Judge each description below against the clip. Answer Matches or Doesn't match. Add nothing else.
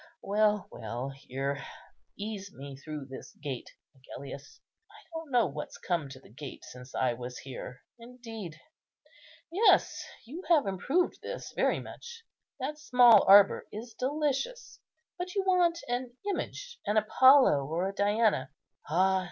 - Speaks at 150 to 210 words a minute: Doesn't match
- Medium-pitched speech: Doesn't match